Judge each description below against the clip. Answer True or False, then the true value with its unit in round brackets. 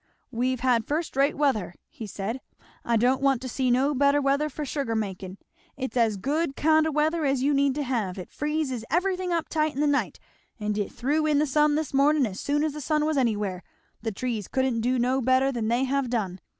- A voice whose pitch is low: False (265 Hz)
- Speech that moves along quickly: True (225 wpm)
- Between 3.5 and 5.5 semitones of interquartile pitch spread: True (4.3 semitones)